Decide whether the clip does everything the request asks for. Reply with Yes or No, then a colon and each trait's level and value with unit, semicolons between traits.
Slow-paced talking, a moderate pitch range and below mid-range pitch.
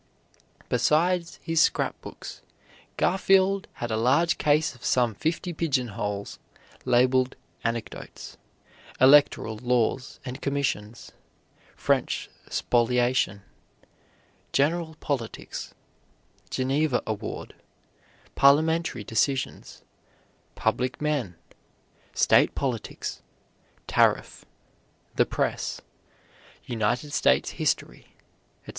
Yes: slow, 75 wpm; average, 4.6 semitones; low, 130 Hz